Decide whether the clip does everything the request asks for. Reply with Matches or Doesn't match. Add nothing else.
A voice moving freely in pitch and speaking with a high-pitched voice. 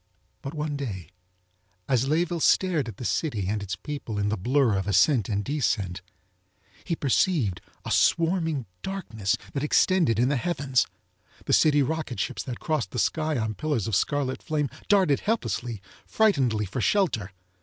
Doesn't match